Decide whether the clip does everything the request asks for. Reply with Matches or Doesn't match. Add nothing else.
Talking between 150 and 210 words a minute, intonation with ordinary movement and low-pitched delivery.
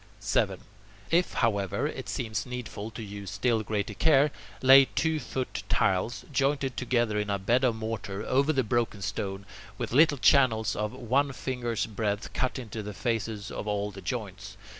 Matches